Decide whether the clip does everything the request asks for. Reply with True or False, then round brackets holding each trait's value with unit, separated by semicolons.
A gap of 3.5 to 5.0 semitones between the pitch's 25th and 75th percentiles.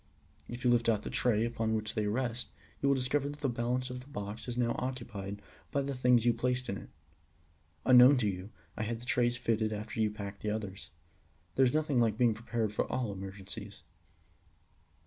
False (2.8 semitones)